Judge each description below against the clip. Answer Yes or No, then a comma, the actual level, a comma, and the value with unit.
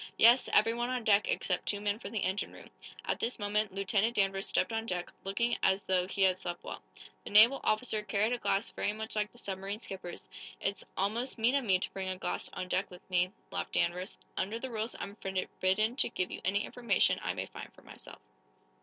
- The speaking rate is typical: No, fast, 215 wpm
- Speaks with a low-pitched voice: No, high, 205 Hz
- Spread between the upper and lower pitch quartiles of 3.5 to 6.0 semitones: No, average, 2.9 semitones